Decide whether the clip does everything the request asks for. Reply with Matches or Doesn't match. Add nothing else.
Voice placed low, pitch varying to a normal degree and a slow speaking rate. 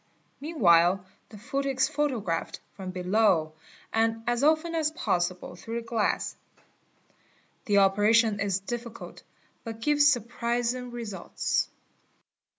Doesn't match